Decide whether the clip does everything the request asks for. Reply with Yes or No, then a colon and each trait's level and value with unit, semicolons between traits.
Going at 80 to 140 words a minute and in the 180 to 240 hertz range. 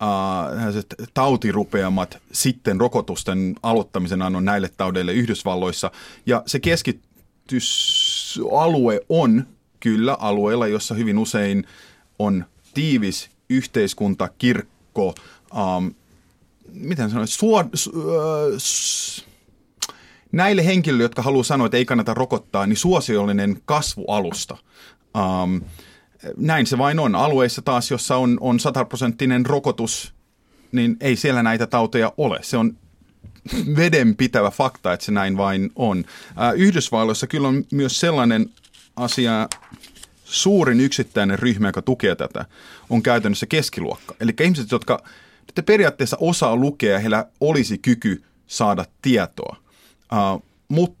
No: average, 115 wpm; low, 120 Hz